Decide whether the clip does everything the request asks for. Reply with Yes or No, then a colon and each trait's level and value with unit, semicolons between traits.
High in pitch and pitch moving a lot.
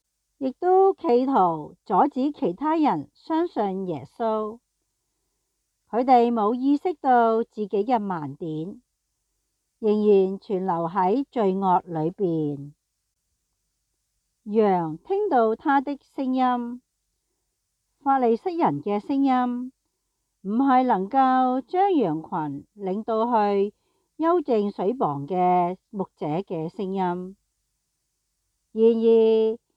Yes: high, 220 Hz; wide, 5.8 semitones